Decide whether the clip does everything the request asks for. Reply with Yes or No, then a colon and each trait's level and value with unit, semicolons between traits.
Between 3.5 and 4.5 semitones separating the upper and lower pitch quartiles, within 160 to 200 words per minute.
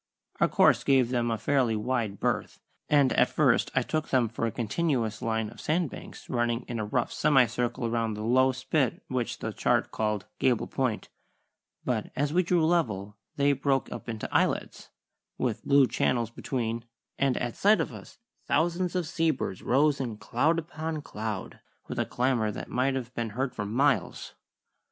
Yes: average, 3.9 semitones; average, 175 wpm